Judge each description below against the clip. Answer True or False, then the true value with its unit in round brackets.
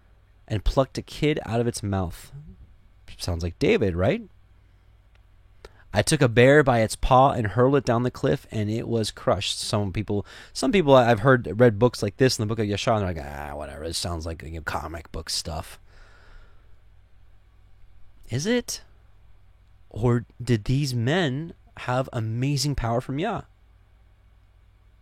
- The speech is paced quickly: False (160 wpm)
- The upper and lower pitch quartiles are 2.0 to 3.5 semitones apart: False (4.4 semitones)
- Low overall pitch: True (100 Hz)